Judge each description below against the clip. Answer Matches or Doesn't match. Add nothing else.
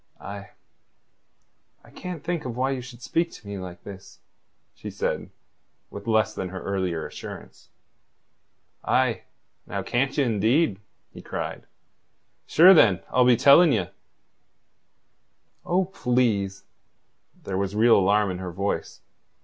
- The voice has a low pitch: Matches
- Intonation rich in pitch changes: Doesn't match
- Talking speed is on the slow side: Matches